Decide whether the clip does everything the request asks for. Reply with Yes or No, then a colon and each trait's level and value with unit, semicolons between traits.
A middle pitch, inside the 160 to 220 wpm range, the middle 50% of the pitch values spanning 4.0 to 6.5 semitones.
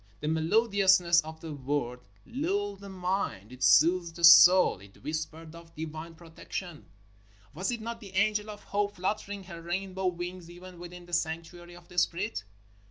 No: medium, 175 Hz; average, 165 wpm; average, 3.2 semitones